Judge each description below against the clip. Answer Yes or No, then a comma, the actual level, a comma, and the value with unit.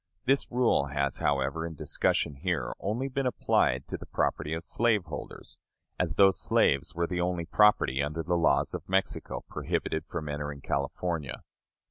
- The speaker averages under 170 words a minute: Yes, average, 155 wpm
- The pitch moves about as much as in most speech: Yes, average, 4.9 semitones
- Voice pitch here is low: Yes, very low, 80 Hz